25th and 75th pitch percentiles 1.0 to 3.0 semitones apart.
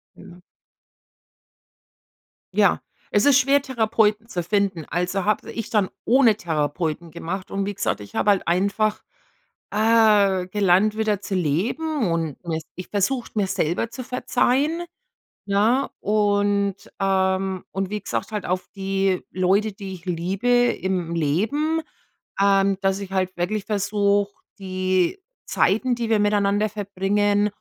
Yes: narrow, 2.5 semitones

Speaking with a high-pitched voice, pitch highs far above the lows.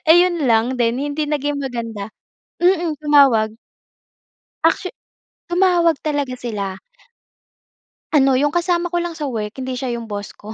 Yes: very high, 280 Hz; wide, 6.0 semitones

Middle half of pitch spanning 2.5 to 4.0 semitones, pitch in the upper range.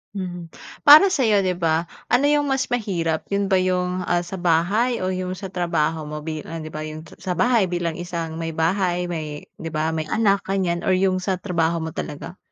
No: average, 2.9 semitones; medium, 180 Hz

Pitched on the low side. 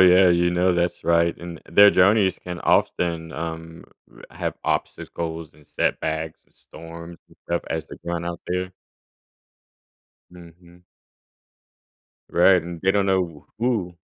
Yes: very low, 85 Hz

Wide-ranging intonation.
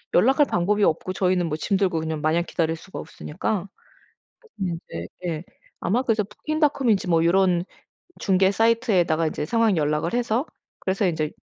No: average, 4.7 semitones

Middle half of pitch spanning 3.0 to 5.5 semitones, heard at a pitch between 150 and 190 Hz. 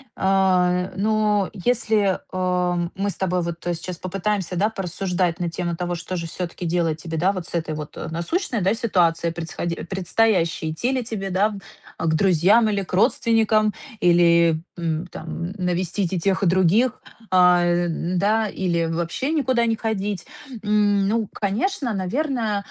Yes: average, 3.5 semitones; medium, 185 Hz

